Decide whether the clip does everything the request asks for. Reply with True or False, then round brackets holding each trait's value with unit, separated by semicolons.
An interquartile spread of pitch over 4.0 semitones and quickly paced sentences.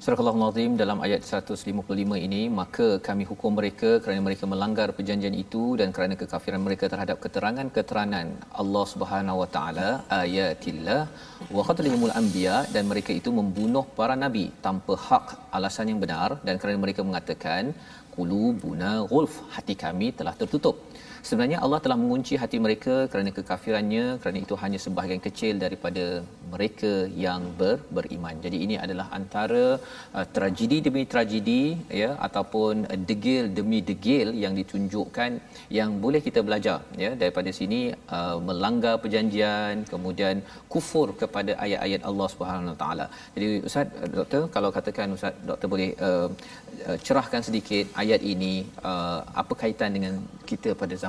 False (3.3 semitones; 140 wpm)